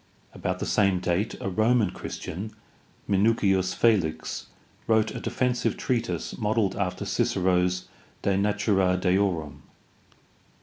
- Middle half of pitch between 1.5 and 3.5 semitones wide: Yes, average, 3.0 semitones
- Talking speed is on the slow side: Yes, slow, 105 wpm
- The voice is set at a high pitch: No, low, 100 Hz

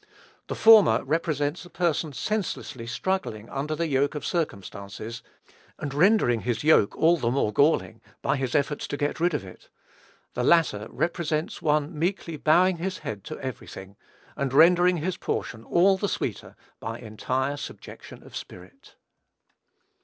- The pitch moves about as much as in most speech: No, wide, 5.9 semitones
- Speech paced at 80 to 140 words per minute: No, average, 155 wpm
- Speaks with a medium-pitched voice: Yes, medium, 150 Hz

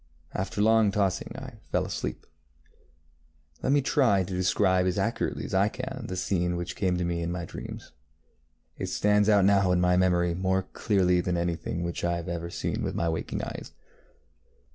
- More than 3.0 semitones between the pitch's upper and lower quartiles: No, narrow, 2.5 semitones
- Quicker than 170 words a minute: Yes, average, 180 wpm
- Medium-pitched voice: No, very low, 90 Hz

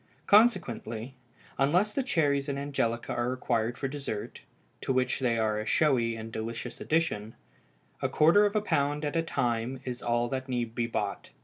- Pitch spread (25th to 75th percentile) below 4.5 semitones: Yes, average, 4.1 semitones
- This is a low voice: Yes, low, 130 Hz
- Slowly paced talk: No, average, 175 wpm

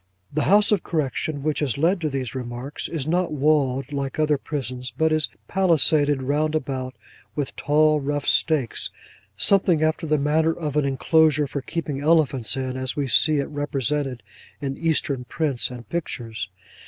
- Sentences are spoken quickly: No, average, 165 wpm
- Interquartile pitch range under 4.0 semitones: Yes, average, 2.8 semitones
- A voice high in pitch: No, medium, 145 Hz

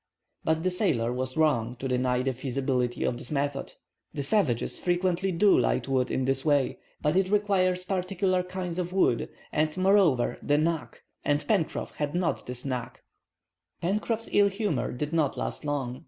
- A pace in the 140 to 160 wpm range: No, average, 170 wpm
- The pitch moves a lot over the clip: Yes, wide, 5.9 semitones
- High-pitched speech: No, medium, 155 Hz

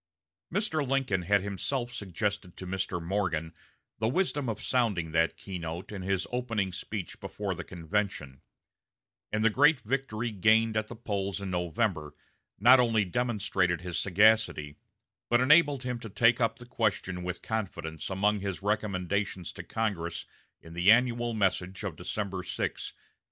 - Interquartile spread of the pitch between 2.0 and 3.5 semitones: No, average, 4.3 semitones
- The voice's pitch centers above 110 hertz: No, low, 100 Hz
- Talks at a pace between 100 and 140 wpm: No, average, 155 wpm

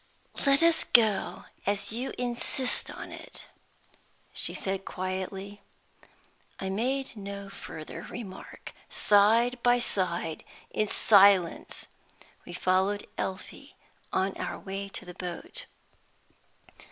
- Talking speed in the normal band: No, slow, 105 wpm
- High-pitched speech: Yes, high, 200 Hz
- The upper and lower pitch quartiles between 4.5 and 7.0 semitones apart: No, average, 4.0 semitones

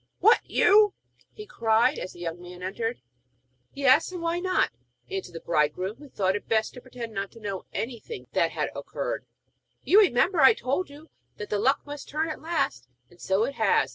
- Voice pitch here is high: Yes, high, 240 Hz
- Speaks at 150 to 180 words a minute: No, average, 195 wpm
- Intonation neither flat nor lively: No, wide, 8.3 semitones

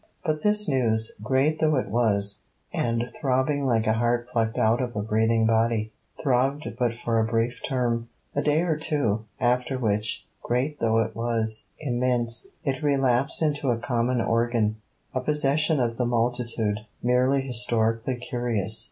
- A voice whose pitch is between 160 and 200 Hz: No, low, 120 Hz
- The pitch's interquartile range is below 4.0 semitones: Yes, average, 2.8 semitones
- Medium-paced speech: Yes, average, 155 wpm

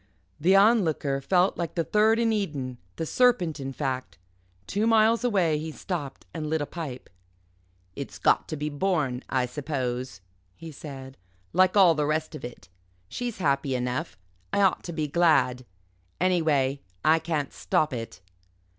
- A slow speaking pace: No, average, 155 wpm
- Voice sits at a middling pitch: Yes, medium, 155 Hz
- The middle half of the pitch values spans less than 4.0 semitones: No, average, 5.3 semitones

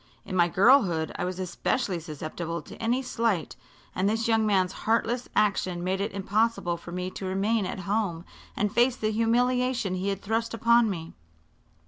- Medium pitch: No, high, 200 Hz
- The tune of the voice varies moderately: Yes, average, 3.9 semitones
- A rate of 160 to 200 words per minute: Yes, average, 170 wpm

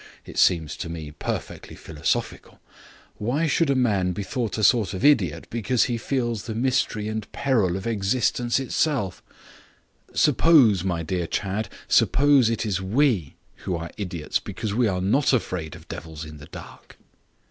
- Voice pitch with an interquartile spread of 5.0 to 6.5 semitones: Yes, wide, 5.6 semitones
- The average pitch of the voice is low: Yes, low, 105 Hz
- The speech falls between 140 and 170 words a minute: Yes, average, 165 wpm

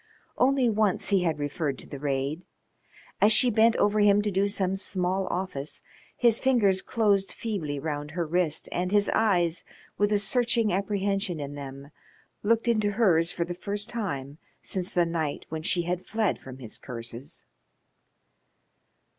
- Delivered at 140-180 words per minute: Yes, average, 160 wpm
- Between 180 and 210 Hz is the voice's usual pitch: Yes, medium, 185 Hz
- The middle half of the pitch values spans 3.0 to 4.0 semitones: No, average, 5.0 semitones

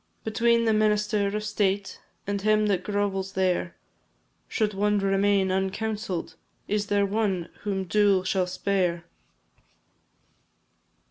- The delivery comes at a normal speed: No, slow, 115 wpm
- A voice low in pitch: No, high, 200 Hz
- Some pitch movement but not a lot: No, narrow, 1.7 semitones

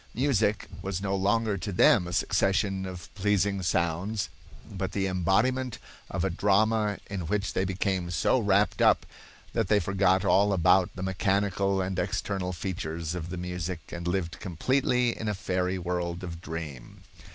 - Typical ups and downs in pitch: No, narrow, 2.3 semitones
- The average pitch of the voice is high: No, very low, 95 Hz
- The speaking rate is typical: Yes, average, 160 wpm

